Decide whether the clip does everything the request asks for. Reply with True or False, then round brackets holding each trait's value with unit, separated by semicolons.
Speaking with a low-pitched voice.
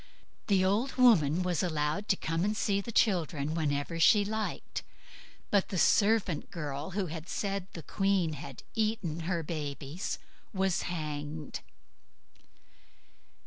False (180 Hz)